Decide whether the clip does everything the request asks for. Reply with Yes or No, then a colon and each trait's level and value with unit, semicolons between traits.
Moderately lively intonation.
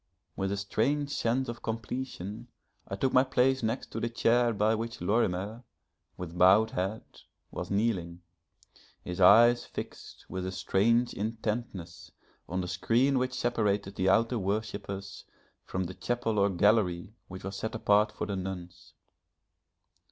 Yes: average, 3.7 semitones